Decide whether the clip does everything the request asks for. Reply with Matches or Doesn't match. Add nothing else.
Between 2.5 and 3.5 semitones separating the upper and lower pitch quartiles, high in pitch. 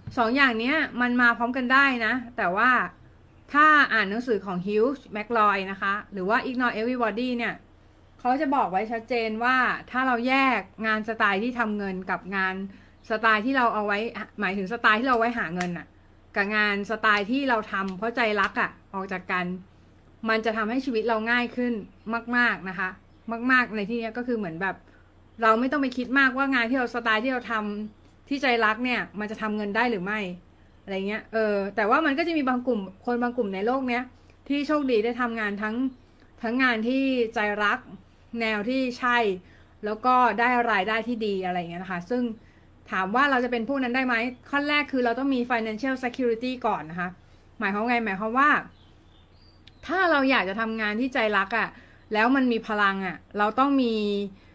Matches